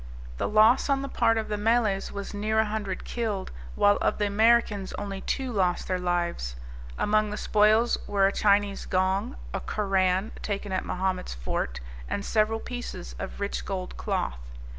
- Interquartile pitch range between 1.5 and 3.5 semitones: Yes, narrow, 2.5 semitones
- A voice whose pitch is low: No, high, 205 Hz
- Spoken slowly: No, average, 170 wpm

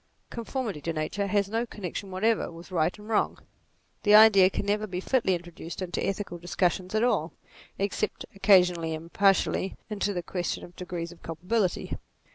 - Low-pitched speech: No, high, 190 Hz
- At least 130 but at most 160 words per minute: No, average, 170 wpm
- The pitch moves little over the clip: No, average, 3.1 semitones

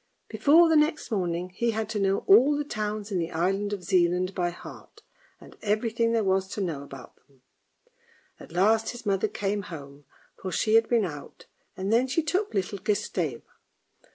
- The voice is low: No, high, 200 Hz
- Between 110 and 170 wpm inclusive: No, average, 180 wpm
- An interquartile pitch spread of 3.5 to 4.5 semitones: Yes, average, 4.1 semitones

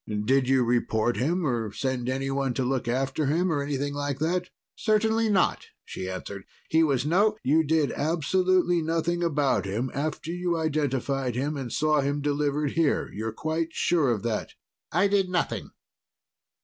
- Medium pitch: Yes, medium, 145 Hz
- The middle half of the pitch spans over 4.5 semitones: No, average, 4.2 semitones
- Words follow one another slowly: No, average, 165 wpm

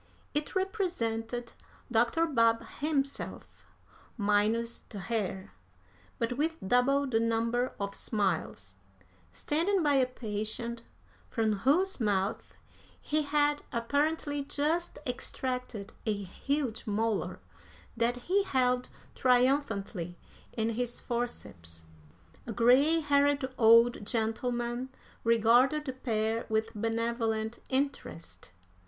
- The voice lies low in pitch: No, high, 240 Hz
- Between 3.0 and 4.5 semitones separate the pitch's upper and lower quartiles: Yes, average, 4.1 semitones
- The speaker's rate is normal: No, slow, 100 wpm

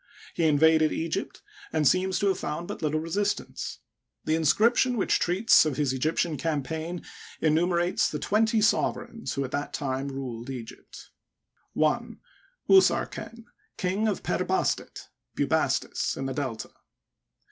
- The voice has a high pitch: No, medium, 160 Hz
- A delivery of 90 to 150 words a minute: Yes, slow, 135 wpm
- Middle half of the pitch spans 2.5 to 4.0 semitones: No, average, 5.2 semitones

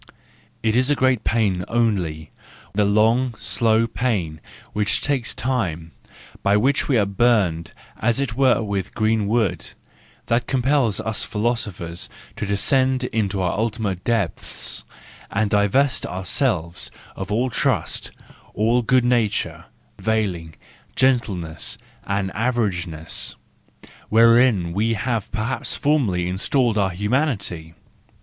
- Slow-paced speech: Yes, slow, 115 wpm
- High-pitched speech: No, low, 110 Hz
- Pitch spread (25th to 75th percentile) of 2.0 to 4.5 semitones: Yes, average, 4.2 semitones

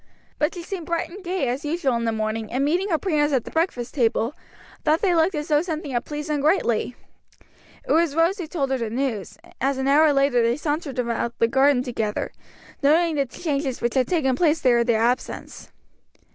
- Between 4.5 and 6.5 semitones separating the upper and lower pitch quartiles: Yes, average, 4.9 semitones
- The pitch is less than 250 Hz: No, very high, 280 Hz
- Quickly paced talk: Yes, fast, 215 wpm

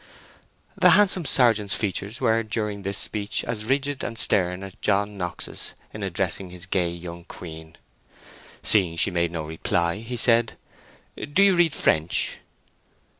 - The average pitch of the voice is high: No, low, 100 Hz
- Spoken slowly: No, average, 145 wpm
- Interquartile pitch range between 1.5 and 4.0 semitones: No, average, 4.6 semitones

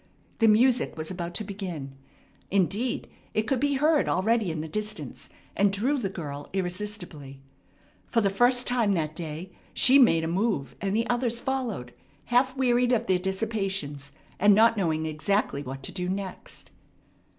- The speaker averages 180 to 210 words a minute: No, average, 160 wpm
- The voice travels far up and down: Yes, wide, 5.8 semitones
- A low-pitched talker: No, high, 200 Hz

